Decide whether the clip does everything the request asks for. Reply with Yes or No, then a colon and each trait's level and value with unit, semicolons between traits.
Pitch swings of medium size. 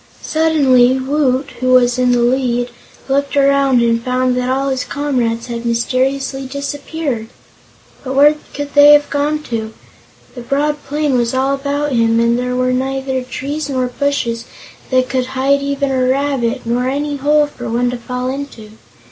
No: narrow, 2.3 semitones